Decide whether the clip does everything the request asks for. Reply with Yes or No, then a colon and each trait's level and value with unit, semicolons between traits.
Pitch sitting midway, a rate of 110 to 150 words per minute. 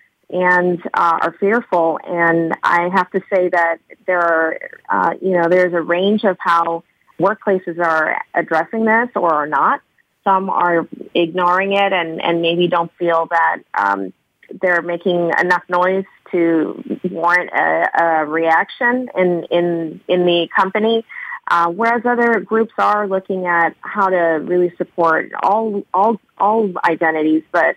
Yes: medium, 175 Hz; average, 145 wpm